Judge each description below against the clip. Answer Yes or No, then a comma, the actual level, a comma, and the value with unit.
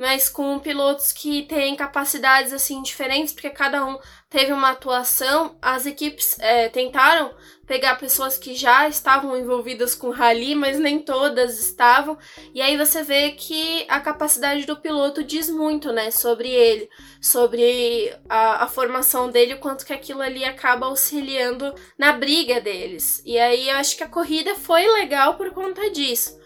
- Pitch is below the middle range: No, very high, 280 Hz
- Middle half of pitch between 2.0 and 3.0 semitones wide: Yes, average, 2.7 semitones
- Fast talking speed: No, average, 165 wpm